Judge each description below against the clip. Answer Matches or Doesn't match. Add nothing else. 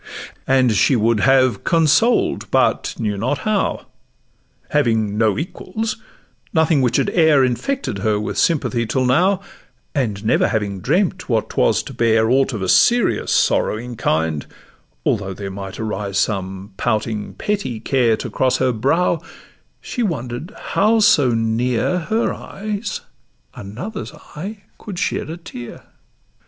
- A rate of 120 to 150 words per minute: Matches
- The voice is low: Matches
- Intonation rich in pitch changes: Matches